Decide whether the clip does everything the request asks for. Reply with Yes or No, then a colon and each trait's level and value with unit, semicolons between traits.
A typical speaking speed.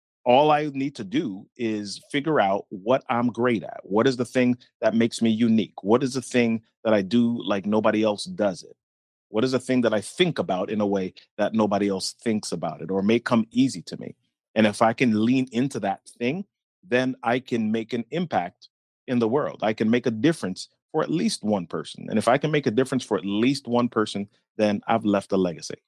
No: fast, 230 wpm